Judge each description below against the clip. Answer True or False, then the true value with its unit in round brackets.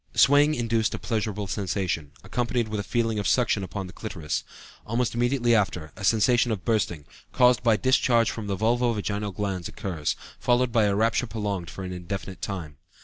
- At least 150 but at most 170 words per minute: False (180 wpm)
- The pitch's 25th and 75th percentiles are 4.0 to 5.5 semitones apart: False (3.6 semitones)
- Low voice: True (105 Hz)